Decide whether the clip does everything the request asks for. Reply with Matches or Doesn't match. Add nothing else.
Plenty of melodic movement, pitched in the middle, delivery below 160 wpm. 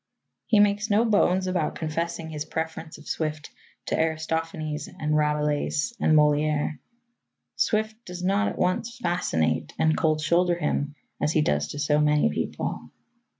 Doesn't match